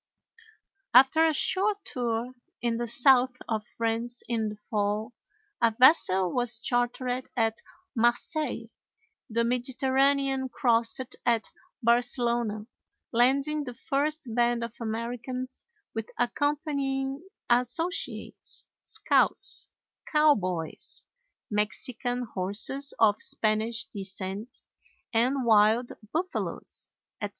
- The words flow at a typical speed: No, slow, 95 wpm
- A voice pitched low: No, high, 240 Hz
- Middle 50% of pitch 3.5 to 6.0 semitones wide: No, average, 3.1 semitones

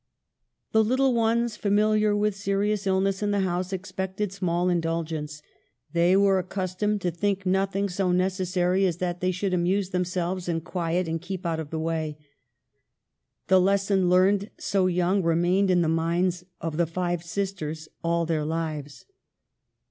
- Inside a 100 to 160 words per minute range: Yes, average, 155 wpm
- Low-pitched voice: No, medium, 185 Hz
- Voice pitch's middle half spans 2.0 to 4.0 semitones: Yes, narrow, 2.6 semitones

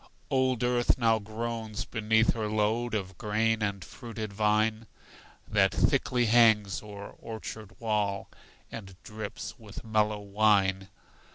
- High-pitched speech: No, low, 110 Hz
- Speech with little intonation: Yes, narrow, 1.6 semitones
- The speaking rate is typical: No, slow, 120 wpm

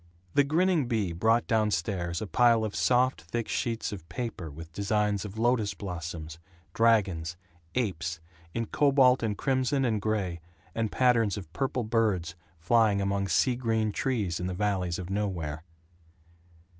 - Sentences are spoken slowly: No, average, 150 wpm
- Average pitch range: Yes, average, 4.7 semitones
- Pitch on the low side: Yes, low, 105 Hz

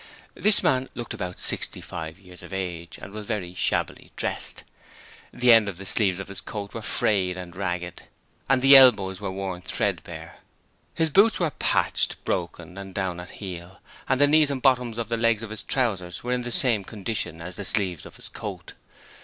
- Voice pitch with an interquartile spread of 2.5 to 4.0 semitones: No, average, 5.0 semitones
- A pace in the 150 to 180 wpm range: No, average, 195 wpm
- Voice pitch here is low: Yes, low, 100 Hz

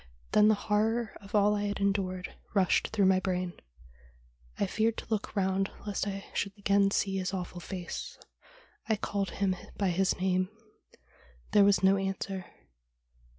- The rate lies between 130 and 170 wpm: Yes, average, 155 wpm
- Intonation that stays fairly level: Yes, narrow, 1.5 semitones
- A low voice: No, high, 195 Hz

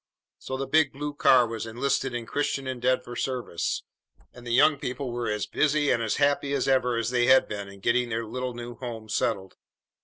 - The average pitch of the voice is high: No, low, 125 Hz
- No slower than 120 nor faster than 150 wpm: No, average, 195 wpm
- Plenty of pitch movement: No, narrow, 2.6 semitones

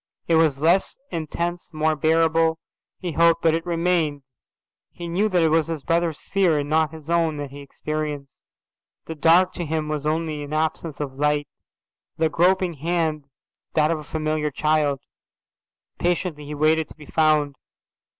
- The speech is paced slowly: No, average, 165 wpm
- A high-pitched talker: No, medium, 160 Hz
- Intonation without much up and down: Yes, narrow, 1.9 semitones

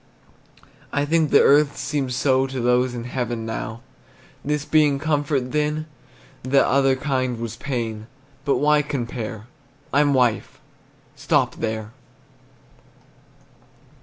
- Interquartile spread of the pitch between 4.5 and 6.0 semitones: No, average, 3.4 semitones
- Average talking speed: No, slow, 115 wpm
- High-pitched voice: No, low, 135 Hz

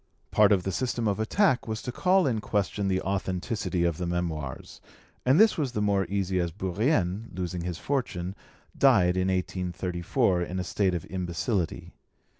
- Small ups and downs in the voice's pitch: No, average, 3.7 semitones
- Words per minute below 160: No, average, 175 wpm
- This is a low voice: Yes, very low, 95 Hz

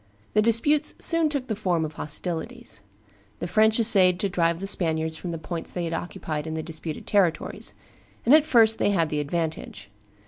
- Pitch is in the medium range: Yes, medium, 175 Hz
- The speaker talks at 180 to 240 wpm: Yes, average, 185 wpm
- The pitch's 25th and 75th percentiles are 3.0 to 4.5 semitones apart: No, wide, 5.5 semitones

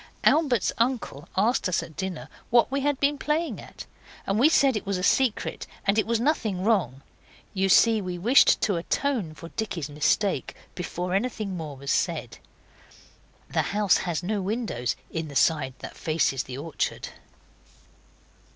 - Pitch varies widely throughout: Yes, wide, 6.1 semitones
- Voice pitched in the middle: No, high, 195 Hz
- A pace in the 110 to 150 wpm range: No, average, 160 wpm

